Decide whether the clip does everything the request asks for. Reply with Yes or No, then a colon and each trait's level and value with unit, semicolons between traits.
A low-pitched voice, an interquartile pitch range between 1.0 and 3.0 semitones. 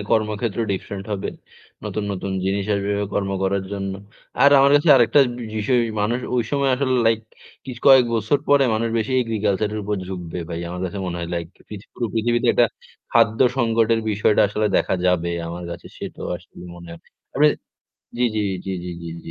No: low, 105 Hz; average, 3.5 semitones